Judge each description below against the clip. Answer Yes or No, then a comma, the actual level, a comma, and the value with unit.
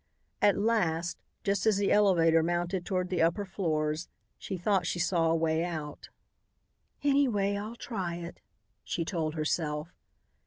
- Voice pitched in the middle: Yes, medium, 175 Hz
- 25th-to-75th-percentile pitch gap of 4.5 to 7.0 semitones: No, average, 3.5 semitones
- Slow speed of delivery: No, average, 145 wpm